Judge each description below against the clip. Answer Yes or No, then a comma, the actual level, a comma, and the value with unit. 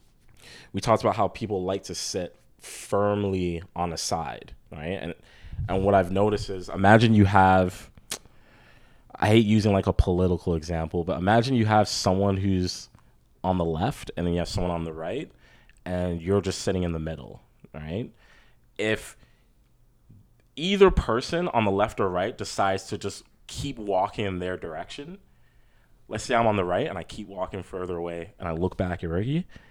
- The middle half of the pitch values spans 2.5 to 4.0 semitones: Yes, average, 3.2 semitones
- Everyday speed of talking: Yes, average, 180 wpm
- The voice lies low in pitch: Yes, very low, 95 Hz